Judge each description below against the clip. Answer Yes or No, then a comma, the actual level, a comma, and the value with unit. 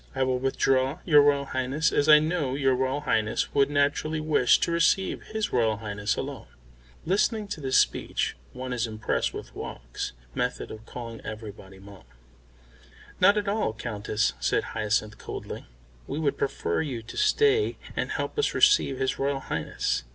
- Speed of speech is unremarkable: Yes, average, 165 wpm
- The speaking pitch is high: No, low, 135 Hz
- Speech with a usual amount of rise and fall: No, wide, 5.7 semitones